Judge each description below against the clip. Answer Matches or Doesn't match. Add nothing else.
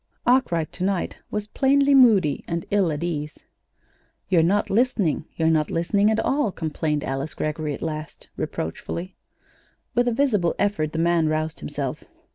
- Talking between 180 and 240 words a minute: Doesn't match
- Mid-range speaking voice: Matches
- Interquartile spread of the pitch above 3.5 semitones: Matches